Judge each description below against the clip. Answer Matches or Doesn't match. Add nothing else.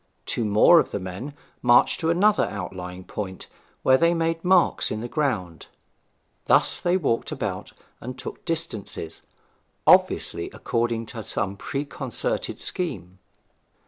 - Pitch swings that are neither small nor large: Doesn't match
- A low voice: Matches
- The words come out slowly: Matches